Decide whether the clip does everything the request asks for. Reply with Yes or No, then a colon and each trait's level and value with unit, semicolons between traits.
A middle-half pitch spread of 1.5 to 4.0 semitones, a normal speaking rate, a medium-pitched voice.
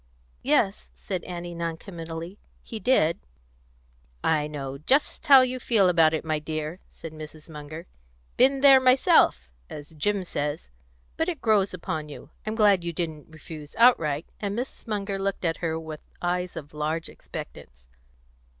No: average, 5.0 semitones; average, 155 wpm; medium, 165 Hz